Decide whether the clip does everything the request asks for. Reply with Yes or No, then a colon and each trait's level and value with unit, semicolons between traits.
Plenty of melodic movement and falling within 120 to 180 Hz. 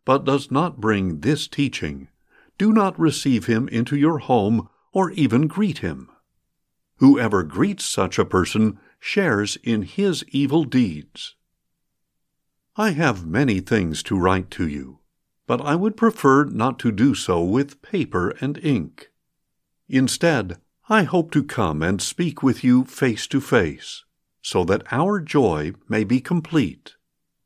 Yes: wide, 6.5 semitones; low, 135 Hz